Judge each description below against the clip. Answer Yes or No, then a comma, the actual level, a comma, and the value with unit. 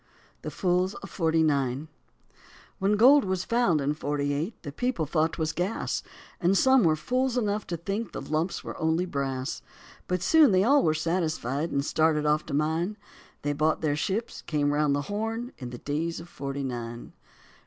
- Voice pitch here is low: No, medium, 160 Hz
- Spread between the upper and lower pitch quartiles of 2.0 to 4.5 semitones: No, average, 5.1 semitones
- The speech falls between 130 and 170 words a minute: No, average, 185 wpm